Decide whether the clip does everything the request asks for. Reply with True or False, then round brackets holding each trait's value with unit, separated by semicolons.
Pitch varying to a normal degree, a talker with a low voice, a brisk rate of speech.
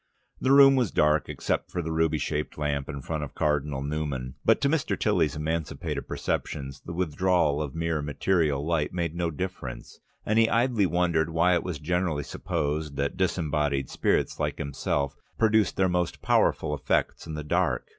False (3.5 semitones; 80 Hz; 175 wpm)